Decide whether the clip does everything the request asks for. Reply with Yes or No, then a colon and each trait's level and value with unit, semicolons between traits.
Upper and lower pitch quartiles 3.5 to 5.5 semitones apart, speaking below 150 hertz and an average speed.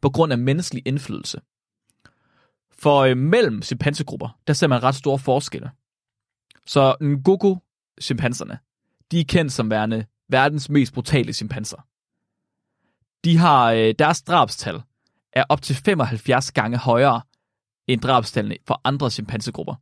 No: average, 4.0 semitones; low, 135 Hz; slow, 125 wpm